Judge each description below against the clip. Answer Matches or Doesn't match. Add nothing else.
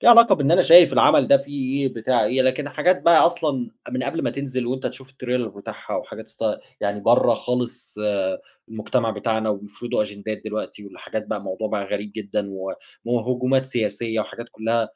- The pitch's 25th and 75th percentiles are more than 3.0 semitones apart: Matches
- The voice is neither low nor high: Doesn't match